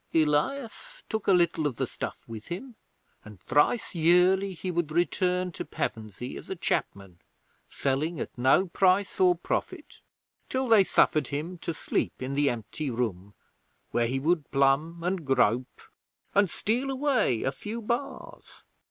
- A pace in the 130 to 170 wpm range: Yes, average, 150 wpm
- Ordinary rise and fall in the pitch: No, wide, 6.3 semitones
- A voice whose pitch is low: No, medium, 165 Hz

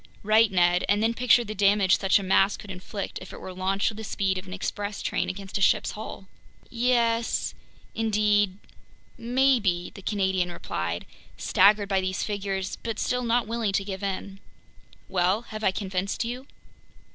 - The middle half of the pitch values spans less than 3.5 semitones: Yes, average, 2.8 semitones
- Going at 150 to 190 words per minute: Yes, average, 170 wpm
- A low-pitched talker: No, high, 200 Hz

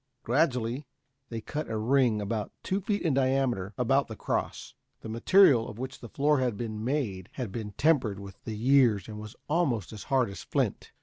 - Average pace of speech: Yes, average, 190 wpm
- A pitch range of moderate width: Yes, average, 4.2 semitones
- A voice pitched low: Yes, low, 120 Hz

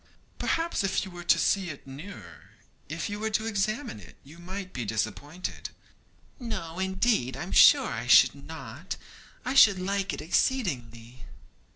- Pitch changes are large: Yes, wide, 6.6 semitones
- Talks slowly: No, average, 155 wpm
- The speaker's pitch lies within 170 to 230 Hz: Yes, medium, 185 Hz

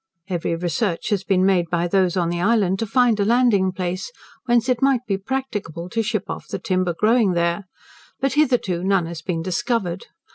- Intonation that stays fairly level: No, average, 4.7 semitones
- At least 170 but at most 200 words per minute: Yes, average, 190 wpm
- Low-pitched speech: No, high, 195 Hz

